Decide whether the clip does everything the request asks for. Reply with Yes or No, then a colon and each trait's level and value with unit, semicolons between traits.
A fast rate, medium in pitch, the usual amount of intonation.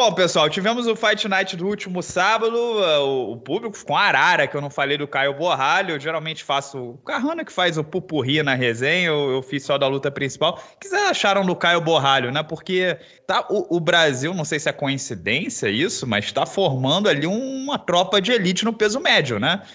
No: fast, 215 wpm; medium, 170 Hz; wide, 6.1 semitones